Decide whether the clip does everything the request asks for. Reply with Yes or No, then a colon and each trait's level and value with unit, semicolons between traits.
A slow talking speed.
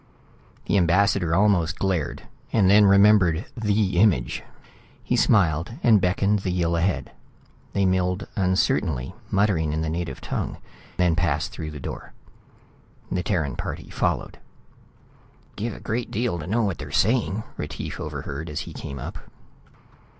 No: average, 145 wpm